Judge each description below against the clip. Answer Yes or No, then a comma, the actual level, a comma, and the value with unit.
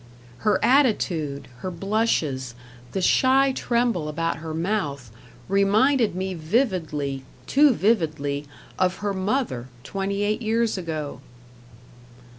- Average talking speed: No, slow, 105 wpm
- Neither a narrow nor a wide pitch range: No, wide, 6.2 semitones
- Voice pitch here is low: No, high, 190 Hz